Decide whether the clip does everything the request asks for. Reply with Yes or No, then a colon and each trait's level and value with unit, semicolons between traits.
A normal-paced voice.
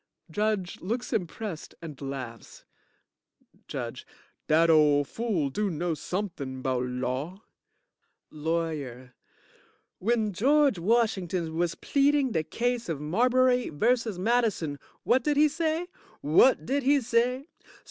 No: slow, 115 wpm